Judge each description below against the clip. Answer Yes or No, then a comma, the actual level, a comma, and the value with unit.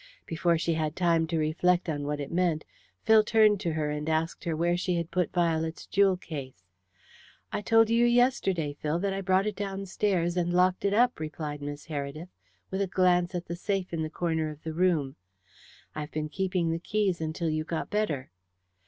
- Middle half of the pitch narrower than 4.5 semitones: Yes, average, 3.3 semitones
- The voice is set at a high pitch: No, medium, 170 Hz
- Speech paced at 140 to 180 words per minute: No, average, 200 wpm